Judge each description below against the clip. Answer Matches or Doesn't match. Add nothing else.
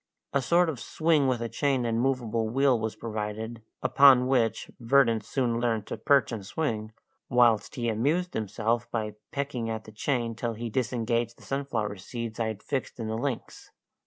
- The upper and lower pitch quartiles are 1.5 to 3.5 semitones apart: Matches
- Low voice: Matches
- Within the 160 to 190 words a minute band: Matches